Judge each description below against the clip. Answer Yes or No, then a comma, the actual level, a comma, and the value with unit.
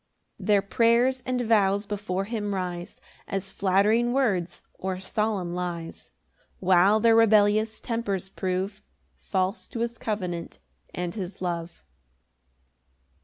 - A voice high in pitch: Yes, high, 200 Hz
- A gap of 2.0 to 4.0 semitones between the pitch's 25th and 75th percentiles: Yes, average, 3.3 semitones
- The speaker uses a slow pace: Yes, slow, 120 wpm